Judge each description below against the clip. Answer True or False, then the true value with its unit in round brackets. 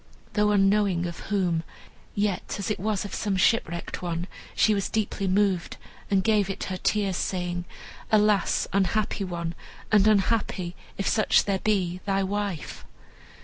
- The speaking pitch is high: True (195 Hz)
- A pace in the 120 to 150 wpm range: True (145 wpm)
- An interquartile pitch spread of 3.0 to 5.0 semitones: False (2.4 semitones)